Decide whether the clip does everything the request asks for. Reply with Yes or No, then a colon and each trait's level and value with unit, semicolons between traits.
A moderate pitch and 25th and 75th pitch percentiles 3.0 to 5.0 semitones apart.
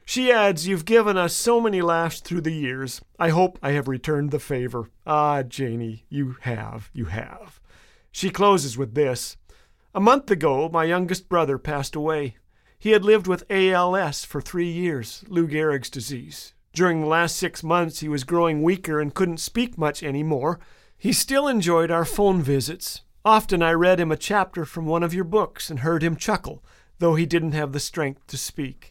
Yes: medium, 165 Hz; average, 4.1 semitones